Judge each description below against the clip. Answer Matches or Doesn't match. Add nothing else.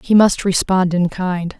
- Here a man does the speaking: Doesn't match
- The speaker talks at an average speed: Matches